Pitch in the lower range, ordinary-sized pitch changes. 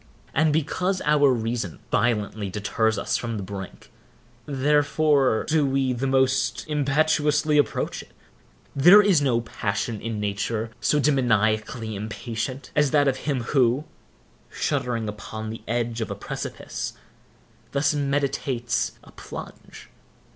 Yes: low, 130 Hz; average, 4.7 semitones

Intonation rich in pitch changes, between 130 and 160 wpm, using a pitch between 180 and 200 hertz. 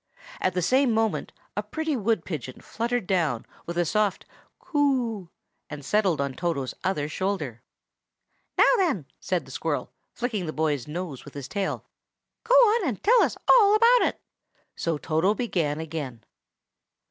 Yes: wide, 8.1 semitones; average, 155 wpm; medium, 185 Hz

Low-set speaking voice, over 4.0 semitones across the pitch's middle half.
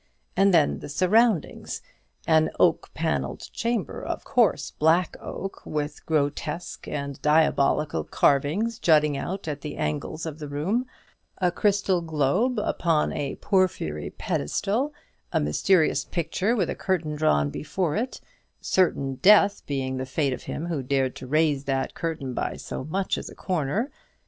No: medium, 155 Hz; average, 5.1 semitones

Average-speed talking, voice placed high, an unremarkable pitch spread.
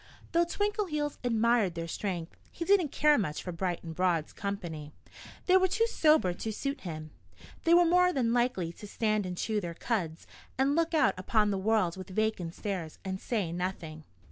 No: average, 185 wpm; high, 210 Hz; wide, 8.9 semitones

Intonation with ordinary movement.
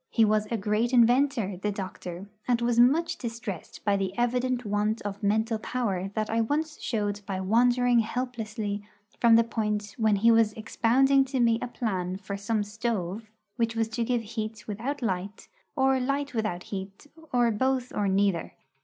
Yes: average, 3.0 semitones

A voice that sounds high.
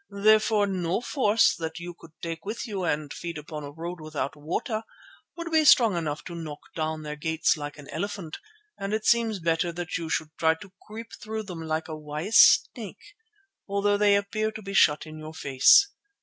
No: medium, 170 Hz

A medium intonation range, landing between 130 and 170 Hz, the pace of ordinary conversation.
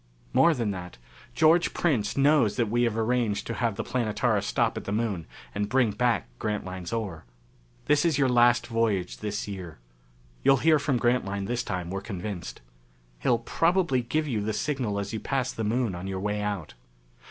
No: average, 3.9 semitones; low, 115 Hz; average, 185 wpm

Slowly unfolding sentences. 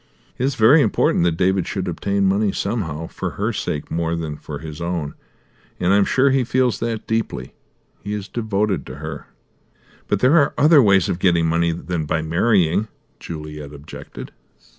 No: average, 175 wpm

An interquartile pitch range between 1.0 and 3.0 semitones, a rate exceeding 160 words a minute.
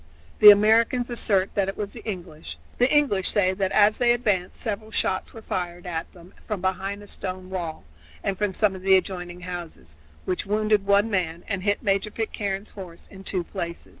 Yes: narrow, 2.5 semitones; average, 195 wpm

